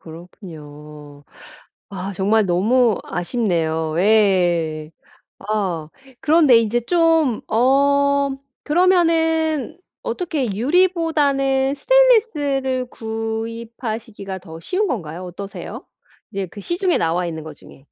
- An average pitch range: No, wide, 8.3 semitones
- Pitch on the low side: No, high, 225 Hz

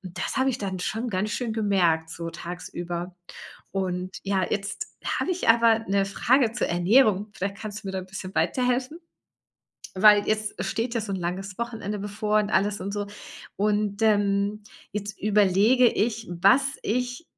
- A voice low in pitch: No, high, 205 Hz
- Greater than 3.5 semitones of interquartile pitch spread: No, average, 2.9 semitones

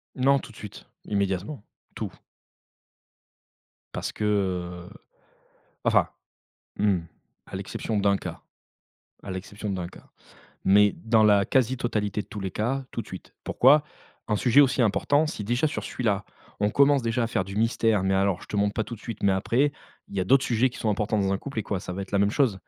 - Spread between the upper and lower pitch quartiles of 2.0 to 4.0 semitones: Yes, average, 3.6 semitones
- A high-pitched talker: No, low, 105 Hz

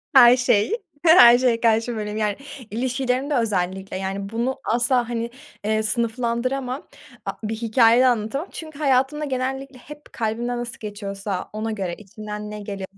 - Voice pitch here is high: Yes, high, 235 Hz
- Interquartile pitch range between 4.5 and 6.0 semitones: No, average, 3.3 semitones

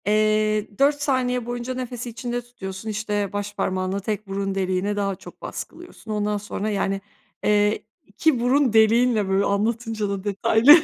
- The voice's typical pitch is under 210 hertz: No, high, 215 Hz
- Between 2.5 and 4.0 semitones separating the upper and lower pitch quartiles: Yes, average, 3.2 semitones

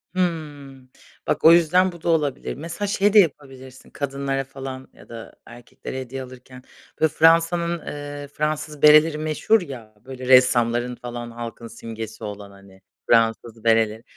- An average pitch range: Yes, average, 4.7 semitones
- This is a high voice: No, low, 135 Hz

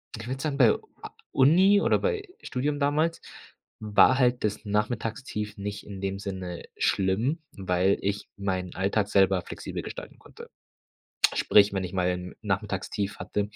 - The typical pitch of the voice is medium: No, low, 105 Hz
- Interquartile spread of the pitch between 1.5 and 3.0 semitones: No, average, 4.9 semitones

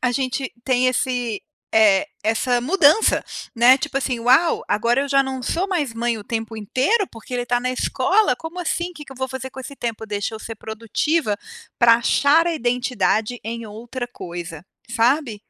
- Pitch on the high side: Yes, high, 245 Hz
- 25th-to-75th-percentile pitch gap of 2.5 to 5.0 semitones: Yes, average, 3.5 semitones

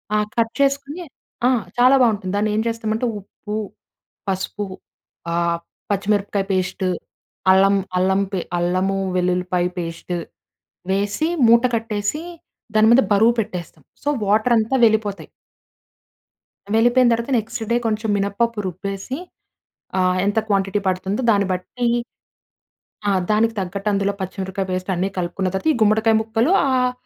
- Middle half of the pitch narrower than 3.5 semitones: Yes, average, 3.1 semitones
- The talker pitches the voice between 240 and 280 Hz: No, high, 205 Hz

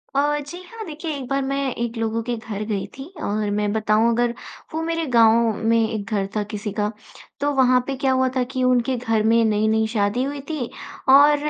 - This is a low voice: No, high, 235 Hz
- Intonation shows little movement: No, average, 4.1 semitones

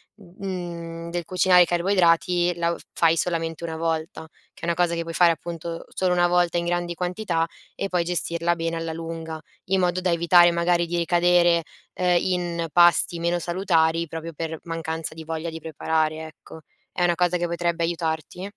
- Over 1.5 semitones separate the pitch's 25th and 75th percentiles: No, narrow, 1.2 semitones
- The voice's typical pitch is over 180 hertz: No, medium, 170 Hz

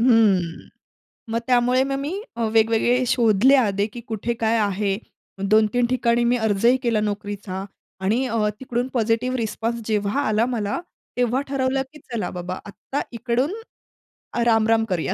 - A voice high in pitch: Yes, high, 230 Hz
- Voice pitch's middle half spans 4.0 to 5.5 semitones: No, average, 3.0 semitones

